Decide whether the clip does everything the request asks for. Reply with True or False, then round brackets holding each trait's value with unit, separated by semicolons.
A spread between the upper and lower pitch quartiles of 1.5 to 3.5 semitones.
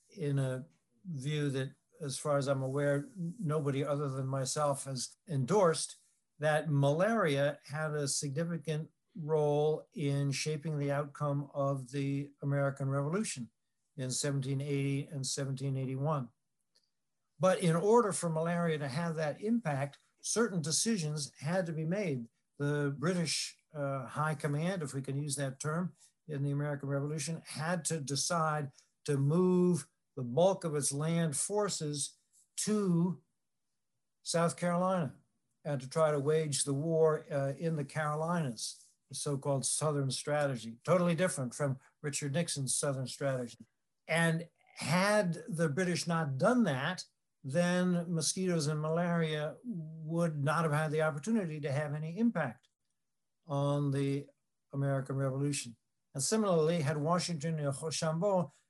True (3.1 semitones)